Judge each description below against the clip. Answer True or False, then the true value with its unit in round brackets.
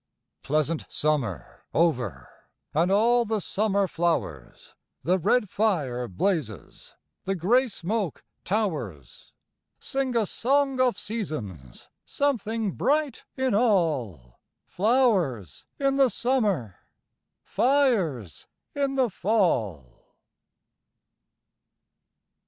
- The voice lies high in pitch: True (195 Hz)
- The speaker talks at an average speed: False (90 wpm)